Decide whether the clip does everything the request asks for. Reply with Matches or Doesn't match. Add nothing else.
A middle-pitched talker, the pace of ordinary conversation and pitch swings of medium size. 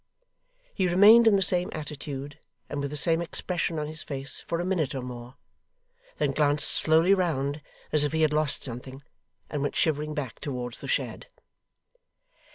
Matches